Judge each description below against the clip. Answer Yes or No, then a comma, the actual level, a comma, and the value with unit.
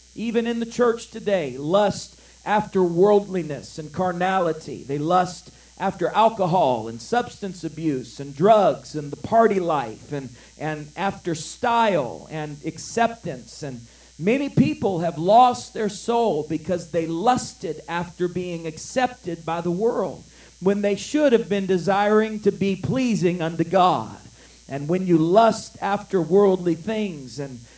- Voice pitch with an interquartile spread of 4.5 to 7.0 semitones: Yes, average, 4.9 semitones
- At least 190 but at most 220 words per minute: No, average, 140 wpm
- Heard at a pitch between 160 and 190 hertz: Yes, medium, 185 Hz